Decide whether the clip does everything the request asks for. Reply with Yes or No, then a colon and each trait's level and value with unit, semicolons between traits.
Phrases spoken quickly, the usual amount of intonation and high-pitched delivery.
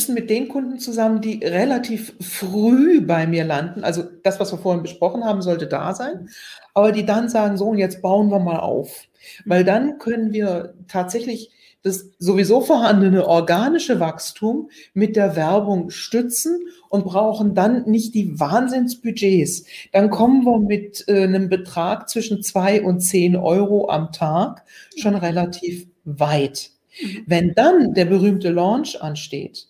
No: average, 145 wpm; average, 4.1 semitones; high, 200 Hz